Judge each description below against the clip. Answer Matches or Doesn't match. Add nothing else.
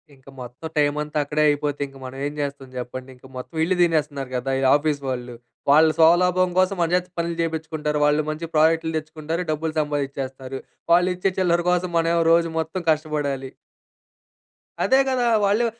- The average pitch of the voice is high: Doesn't match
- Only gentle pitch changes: Doesn't match